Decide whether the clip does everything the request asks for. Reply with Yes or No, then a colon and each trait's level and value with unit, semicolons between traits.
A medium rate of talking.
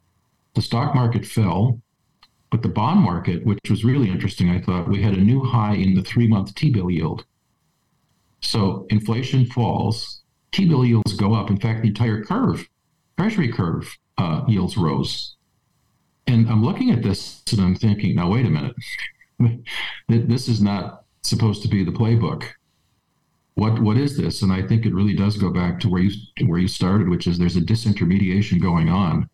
Yes: average, 175 wpm